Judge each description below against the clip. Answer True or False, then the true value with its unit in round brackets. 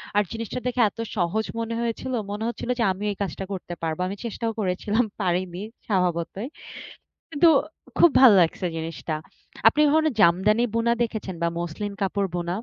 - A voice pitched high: True (205 Hz)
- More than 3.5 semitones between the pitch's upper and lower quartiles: True (4.4 semitones)